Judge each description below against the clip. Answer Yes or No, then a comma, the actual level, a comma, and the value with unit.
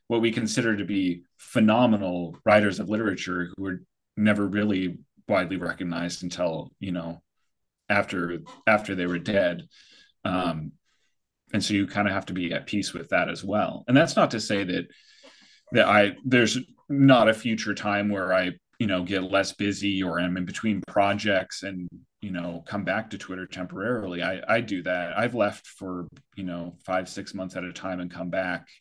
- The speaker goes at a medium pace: Yes, average, 185 wpm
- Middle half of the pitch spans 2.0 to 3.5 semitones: Yes, average, 2.7 semitones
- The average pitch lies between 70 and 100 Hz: Yes, very low, 95 Hz